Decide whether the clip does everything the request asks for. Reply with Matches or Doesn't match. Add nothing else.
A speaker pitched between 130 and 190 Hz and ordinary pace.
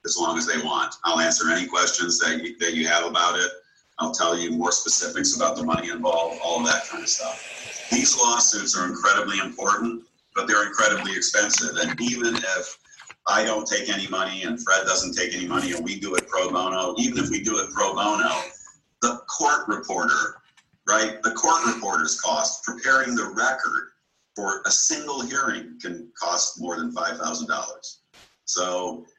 Doesn't match